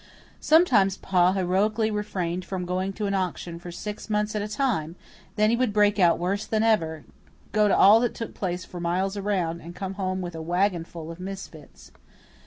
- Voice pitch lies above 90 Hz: Yes, high, 190 Hz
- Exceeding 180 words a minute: Yes, average, 190 wpm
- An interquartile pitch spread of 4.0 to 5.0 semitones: No, average, 3.1 semitones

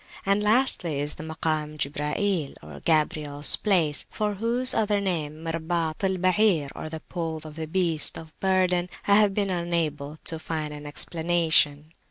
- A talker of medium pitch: Yes, medium, 165 Hz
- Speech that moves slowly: No, average, 150 wpm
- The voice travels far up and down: No, average, 3.8 semitones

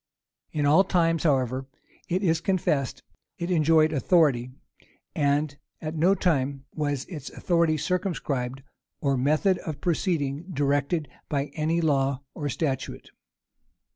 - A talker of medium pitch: Yes, medium, 150 Hz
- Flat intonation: No, average, 3.3 semitones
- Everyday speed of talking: No, slow, 120 wpm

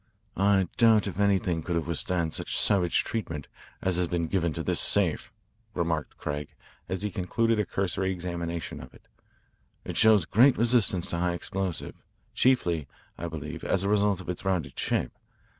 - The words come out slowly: No, average, 170 wpm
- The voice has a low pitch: Yes, very low, 90 Hz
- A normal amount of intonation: Yes, average, 3.1 semitones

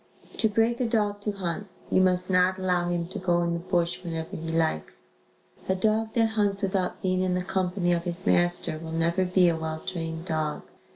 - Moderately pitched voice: Yes, medium, 180 Hz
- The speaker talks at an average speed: No, fast, 210 wpm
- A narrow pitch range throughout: Yes, narrow, 2.2 semitones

